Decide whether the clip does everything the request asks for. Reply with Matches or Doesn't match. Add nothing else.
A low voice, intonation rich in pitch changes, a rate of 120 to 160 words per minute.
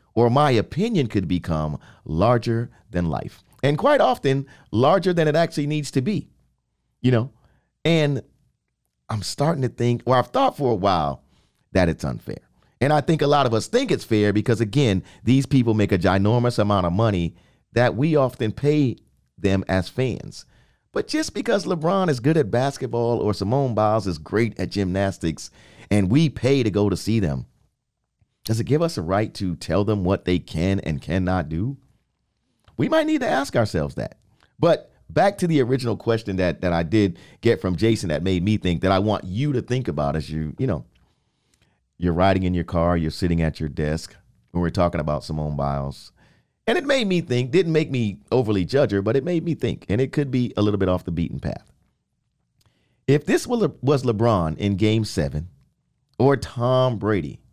Doesn't match